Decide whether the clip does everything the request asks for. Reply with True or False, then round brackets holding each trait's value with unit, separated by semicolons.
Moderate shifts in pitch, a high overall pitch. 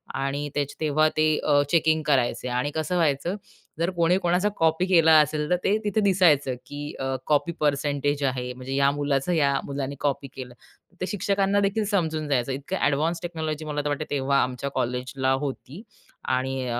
False (3.3 semitones; 145 Hz)